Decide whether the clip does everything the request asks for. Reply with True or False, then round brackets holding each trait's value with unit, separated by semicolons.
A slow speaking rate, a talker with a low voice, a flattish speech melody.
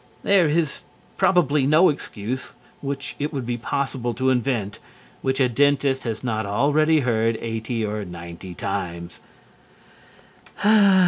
False (125 wpm; 125 Hz; 4.7 semitones)